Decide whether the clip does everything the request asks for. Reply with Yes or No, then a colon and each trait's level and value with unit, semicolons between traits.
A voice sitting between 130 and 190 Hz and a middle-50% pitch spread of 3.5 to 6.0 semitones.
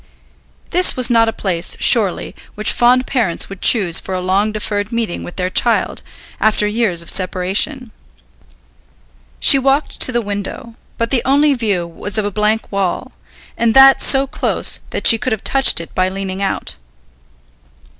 No: high, 215 Hz; average, 4.2 semitones